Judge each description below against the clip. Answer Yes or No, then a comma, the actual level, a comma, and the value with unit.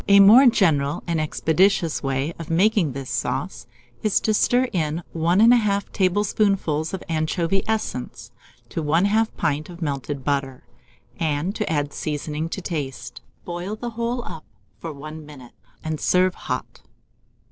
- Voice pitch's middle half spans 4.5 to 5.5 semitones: Yes, average, 5.1 semitones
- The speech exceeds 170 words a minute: No, average, 145 wpm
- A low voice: No, medium, 165 Hz